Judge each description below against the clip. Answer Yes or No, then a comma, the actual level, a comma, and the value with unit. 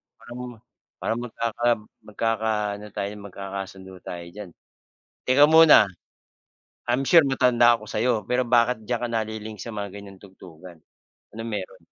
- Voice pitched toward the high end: No, low, 110 Hz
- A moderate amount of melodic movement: Yes, average, 3.3 semitones